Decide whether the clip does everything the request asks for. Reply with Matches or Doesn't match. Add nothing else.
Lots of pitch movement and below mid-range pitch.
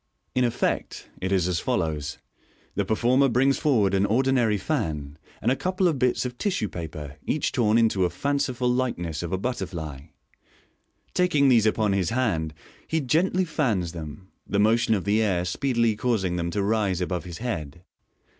Matches